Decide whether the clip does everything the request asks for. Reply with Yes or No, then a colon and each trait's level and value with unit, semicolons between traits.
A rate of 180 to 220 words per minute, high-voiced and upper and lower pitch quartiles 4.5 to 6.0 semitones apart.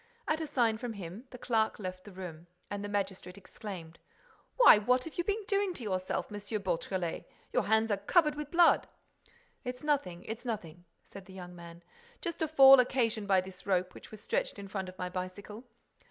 Yes: average, 200 wpm; high, 205 Hz; wide, 5.4 semitones